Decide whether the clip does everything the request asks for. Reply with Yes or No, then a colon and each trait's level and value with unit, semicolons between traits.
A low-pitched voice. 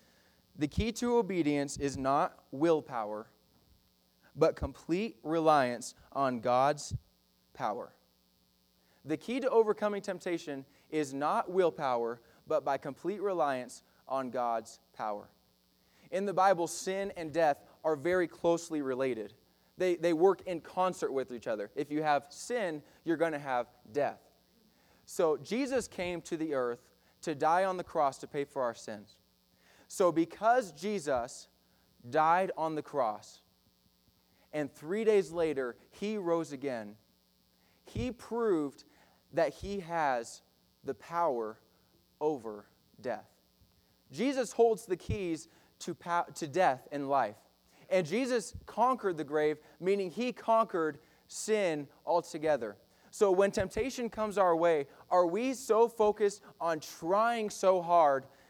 No: medium, 160 Hz